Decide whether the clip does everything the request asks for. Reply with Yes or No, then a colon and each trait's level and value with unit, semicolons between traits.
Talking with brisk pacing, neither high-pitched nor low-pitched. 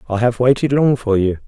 No: fast, 245 wpm; low, 120 Hz